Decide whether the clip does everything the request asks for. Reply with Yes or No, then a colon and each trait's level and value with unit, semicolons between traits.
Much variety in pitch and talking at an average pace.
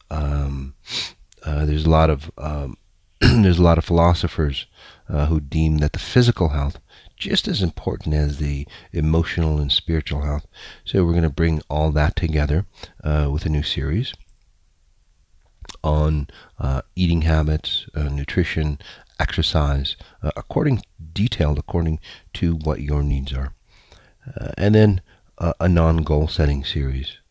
No: average, 2.9 semitones; average, 145 wpm